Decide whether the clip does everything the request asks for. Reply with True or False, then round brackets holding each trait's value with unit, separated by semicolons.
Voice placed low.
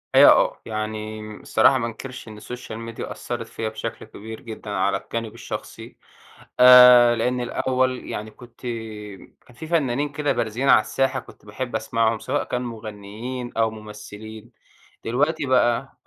True (115 Hz)